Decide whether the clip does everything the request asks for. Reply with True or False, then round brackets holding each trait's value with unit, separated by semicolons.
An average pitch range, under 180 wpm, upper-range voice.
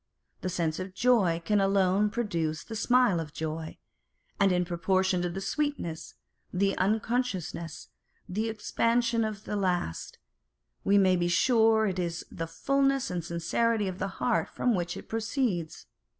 True (4.5 semitones; 150 wpm; 195 Hz)